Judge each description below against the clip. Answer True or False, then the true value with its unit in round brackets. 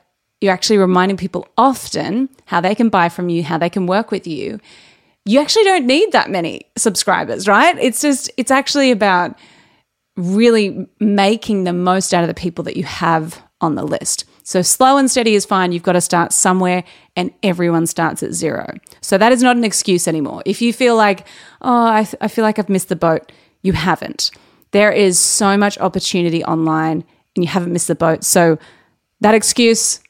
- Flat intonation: False (4.1 semitones)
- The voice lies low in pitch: False (190 Hz)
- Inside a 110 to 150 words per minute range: False (195 wpm)